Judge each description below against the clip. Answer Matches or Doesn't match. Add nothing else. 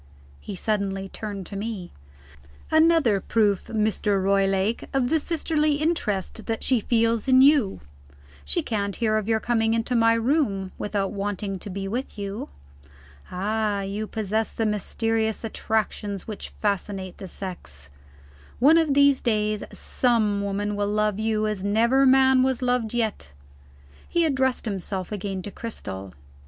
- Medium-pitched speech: Doesn't match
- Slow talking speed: Doesn't match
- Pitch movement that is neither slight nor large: Matches